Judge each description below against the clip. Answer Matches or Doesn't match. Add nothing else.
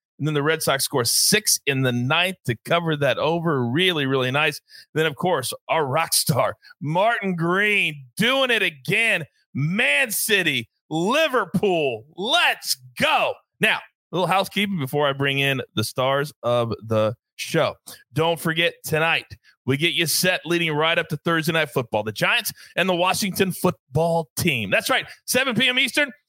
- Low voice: Doesn't match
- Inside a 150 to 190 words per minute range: Matches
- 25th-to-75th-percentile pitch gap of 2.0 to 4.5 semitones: Doesn't match